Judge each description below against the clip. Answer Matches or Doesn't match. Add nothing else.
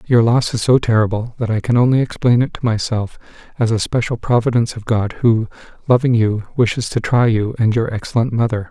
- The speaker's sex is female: Doesn't match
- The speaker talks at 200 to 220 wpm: Matches